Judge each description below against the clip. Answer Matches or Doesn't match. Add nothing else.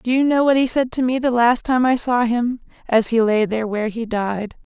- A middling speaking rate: Doesn't match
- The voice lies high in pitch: Matches